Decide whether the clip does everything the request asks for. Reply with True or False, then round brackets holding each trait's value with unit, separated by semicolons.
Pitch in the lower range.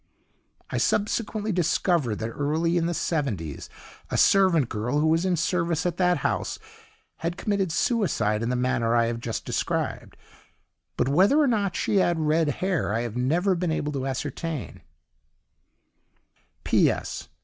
False (160 Hz)